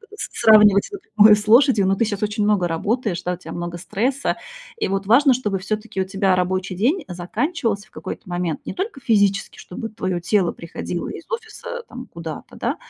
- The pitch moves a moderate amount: Yes, average, 4.3 semitones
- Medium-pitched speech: No, high, 205 Hz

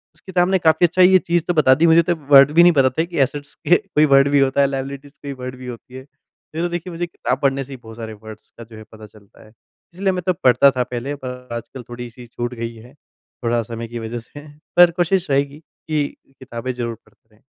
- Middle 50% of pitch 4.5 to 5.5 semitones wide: Yes, average, 5.2 semitones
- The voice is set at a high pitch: No, low, 135 Hz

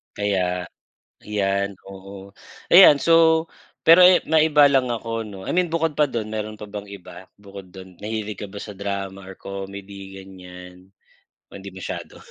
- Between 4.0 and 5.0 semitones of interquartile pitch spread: No, average, 3.0 semitones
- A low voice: Yes, low, 100 Hz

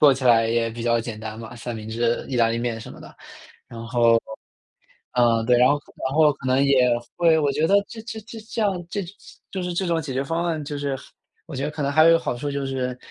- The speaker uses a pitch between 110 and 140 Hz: Yes, low, 135 Hz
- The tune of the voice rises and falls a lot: No, average, 5.0 semitones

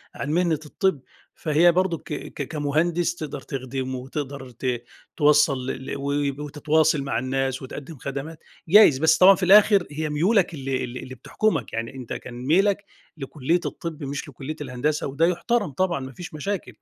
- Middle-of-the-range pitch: Yes, medium, 150 Hz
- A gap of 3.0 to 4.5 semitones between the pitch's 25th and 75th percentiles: Yes, average, 4.1 semitones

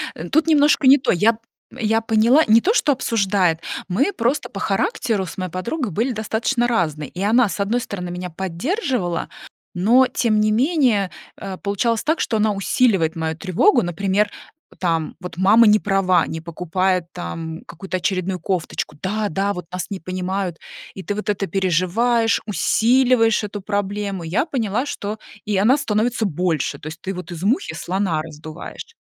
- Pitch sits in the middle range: No, high, 200 Hz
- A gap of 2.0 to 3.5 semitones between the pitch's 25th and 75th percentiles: No, average, 4.2 semitones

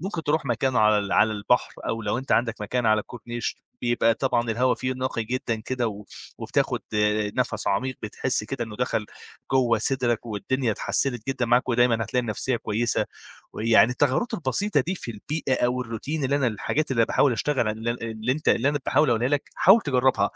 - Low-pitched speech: Yes, low, 120 Hz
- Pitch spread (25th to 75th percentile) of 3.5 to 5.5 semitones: No, average, 2.9 semitones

